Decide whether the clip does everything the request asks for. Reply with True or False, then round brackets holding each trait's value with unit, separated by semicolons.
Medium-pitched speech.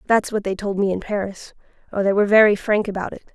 False (200 Hz)